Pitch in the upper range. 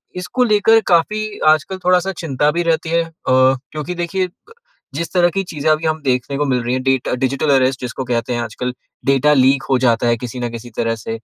No: medium, 140 Hz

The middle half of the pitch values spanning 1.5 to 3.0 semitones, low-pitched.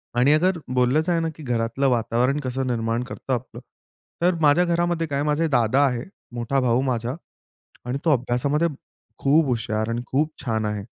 No: average, 4.1 semitones; low, 130 Hz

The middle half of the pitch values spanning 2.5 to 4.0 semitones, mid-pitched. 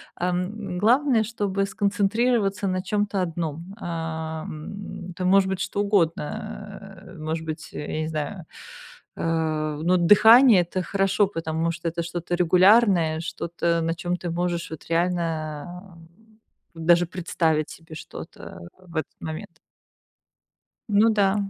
Yes: average, 3.3 semitones; medium, 175 Hz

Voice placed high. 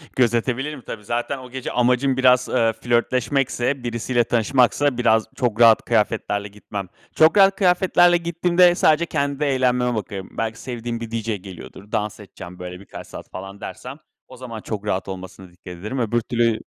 No: low, 120 Hz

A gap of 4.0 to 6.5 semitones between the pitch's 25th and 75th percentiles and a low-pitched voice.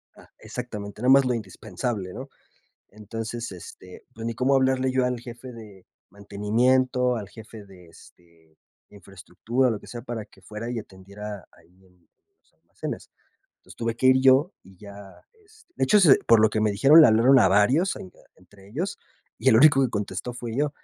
Yes: average, 4.3 semitones; low, 115 Hz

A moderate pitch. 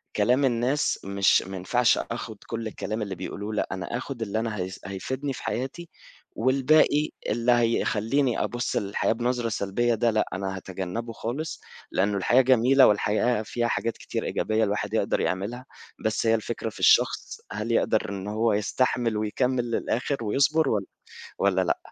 No: low, 115 Hz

